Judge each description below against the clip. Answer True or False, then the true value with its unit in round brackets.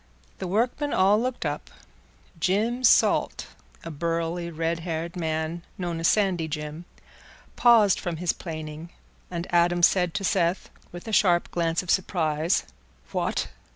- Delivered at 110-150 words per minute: True (140 wpm)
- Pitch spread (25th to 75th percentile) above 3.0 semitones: False (2.6 semitones)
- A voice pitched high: False (175 Hz)